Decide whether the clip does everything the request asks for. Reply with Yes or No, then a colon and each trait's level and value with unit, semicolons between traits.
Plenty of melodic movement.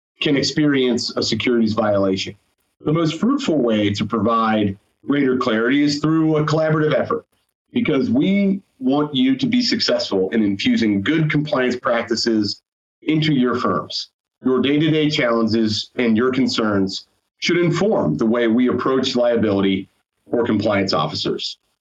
Yes: wide, 5.9 semitones